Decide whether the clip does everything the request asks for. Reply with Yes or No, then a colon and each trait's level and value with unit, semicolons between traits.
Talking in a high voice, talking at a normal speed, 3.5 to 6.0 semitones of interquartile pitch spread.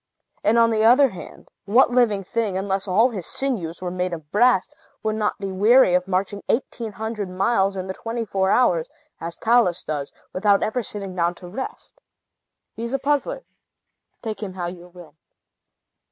Yes: high, 200 Hz; average, 175 wpm; average, 4.1 semitones